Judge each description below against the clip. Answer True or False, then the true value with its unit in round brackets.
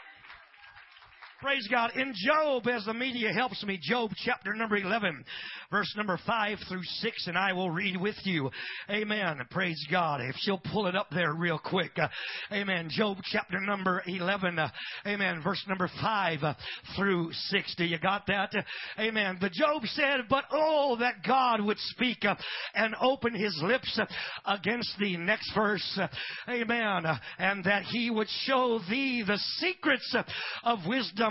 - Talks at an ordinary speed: True (150 wpm)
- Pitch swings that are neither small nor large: True (4.3 semitones)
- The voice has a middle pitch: False (205 Hz)